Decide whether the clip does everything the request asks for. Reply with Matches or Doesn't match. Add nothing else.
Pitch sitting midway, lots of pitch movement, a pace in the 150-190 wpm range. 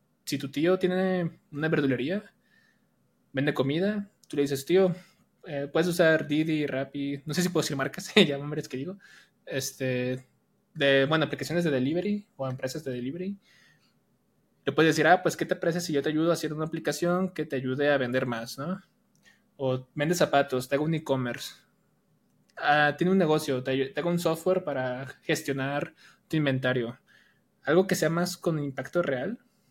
Doesn't match